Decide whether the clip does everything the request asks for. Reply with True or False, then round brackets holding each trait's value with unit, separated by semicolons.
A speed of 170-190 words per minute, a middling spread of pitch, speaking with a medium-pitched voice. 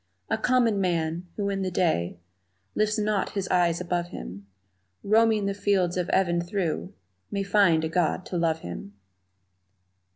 False (155 wpm; 3.2 semitones; 180 Hz)